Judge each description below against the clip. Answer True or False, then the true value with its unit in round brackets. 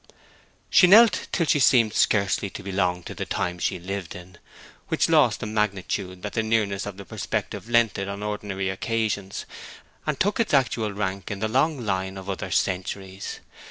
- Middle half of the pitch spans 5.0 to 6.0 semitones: False (2.9 semitones)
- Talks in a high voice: False (100 Hz)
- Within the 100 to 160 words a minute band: False (180 wpm)